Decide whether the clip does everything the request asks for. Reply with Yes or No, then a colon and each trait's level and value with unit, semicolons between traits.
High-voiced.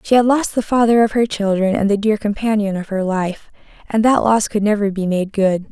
Yes: high, 210 Hz